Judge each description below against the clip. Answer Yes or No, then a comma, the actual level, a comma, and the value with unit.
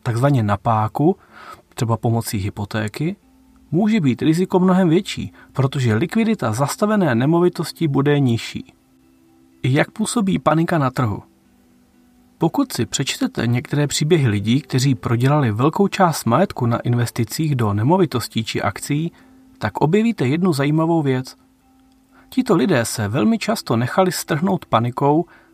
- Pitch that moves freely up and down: Yes, wide, 7.9 semitones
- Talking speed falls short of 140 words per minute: Yes, average, 120 wpm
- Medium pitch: Yes, medium, 145 Hz